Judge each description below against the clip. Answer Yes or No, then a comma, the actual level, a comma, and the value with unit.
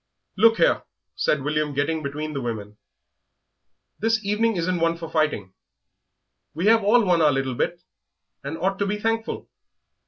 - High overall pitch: No, medium, 165 Hz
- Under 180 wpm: Yes, average, 155 wpm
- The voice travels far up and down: Yes, wide, 6.2 semitones